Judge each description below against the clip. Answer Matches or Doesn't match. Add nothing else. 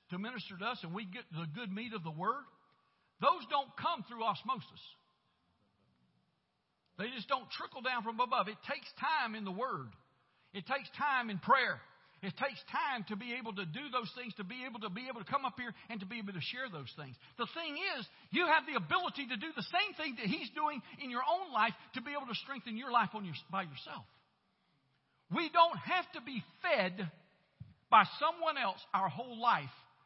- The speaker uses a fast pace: Matches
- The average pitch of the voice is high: Matches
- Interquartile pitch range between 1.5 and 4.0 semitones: Doesn't match